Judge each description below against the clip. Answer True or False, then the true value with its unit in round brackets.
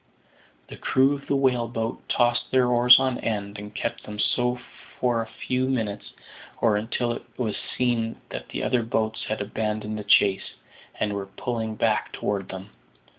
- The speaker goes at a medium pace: True (175 wpm)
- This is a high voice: False (115 Hz)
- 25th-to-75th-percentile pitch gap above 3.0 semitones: False (2.7 semitones)